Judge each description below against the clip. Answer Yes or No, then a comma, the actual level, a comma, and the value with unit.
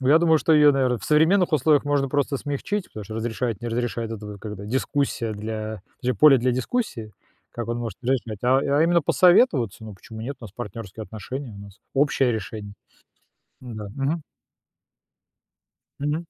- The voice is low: Yes, low, 125 Hz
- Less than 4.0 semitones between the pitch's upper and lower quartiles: No, average, 4.7 semitones